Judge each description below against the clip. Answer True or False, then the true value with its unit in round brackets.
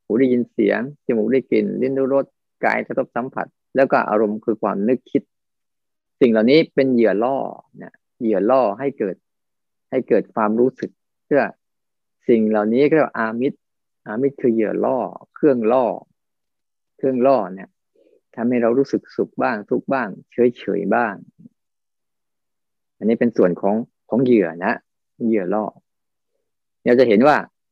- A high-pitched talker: False (120 Hz)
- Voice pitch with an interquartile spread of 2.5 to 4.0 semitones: True (3.4 semitones)